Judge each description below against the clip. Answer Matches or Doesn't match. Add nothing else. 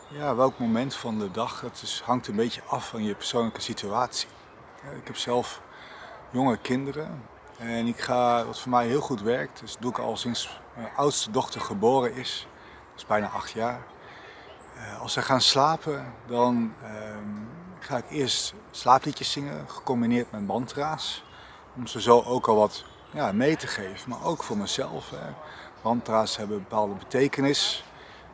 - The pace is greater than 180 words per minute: Doesn't match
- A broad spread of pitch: Doesn't match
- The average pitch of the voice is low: Matches